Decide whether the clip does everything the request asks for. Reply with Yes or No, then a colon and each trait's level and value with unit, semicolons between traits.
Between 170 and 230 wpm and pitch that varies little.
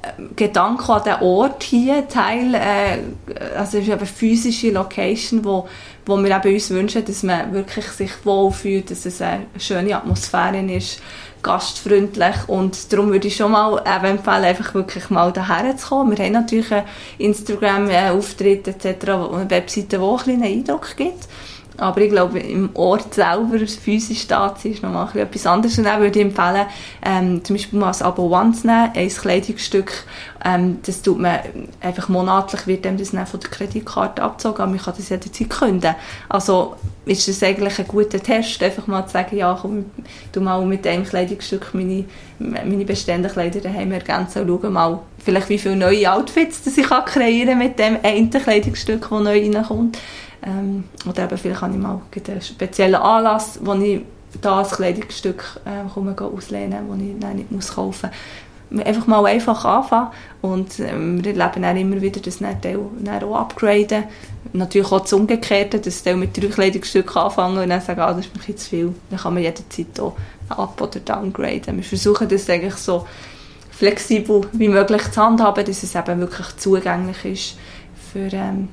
Yes: average, 180 wpm; narrow, 2.3 semitones